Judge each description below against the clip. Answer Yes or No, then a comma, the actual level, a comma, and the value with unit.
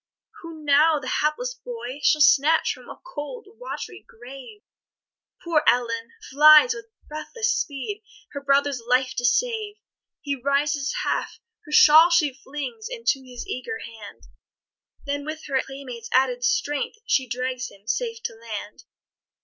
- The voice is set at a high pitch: Yes, very high, 290 Hz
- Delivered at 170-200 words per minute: No, average, 140 wpm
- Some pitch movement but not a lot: No, wide, 7.6 semitones